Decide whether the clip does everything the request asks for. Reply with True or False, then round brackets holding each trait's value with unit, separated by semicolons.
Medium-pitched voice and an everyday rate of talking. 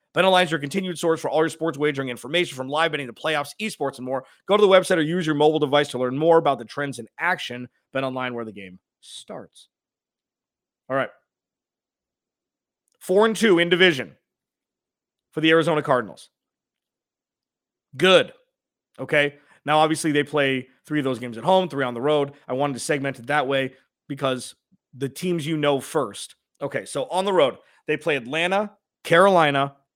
True (150 Hz; 180 wpm)